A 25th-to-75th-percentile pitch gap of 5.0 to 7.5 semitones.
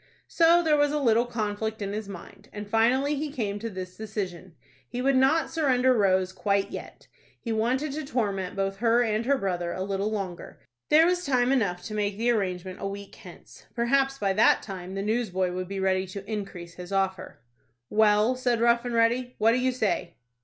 No: average, 4.4 semitones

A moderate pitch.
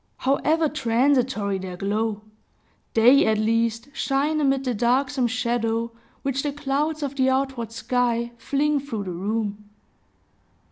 No: high, 245 Hz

